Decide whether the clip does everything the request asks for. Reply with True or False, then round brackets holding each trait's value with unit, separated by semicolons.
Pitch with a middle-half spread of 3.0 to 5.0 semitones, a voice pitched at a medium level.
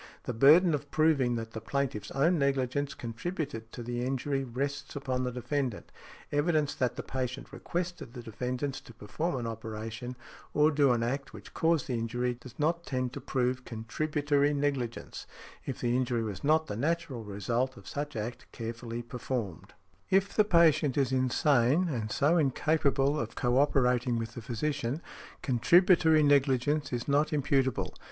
False (3.6 semitones; 130 Hz)